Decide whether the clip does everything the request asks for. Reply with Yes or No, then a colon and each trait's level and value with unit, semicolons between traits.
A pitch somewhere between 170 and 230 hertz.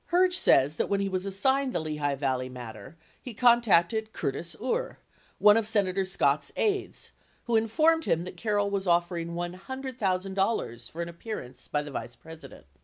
Yes: high, 190 Hz